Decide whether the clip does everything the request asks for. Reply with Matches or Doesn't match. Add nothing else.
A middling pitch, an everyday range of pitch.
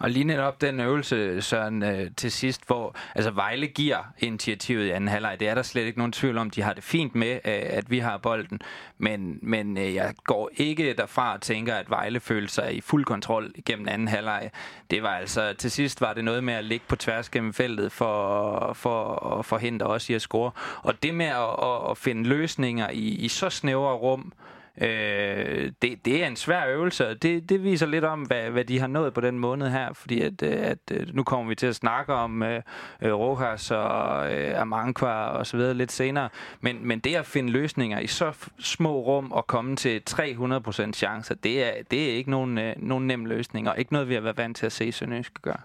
Doesn't match